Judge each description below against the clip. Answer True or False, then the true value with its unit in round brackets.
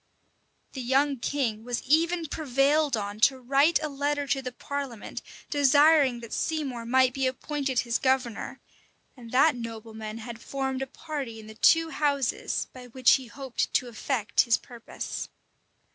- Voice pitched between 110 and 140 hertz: False (260 Hz)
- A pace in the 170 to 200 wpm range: False (160 wpm)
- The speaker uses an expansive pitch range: False (3.3 semitones)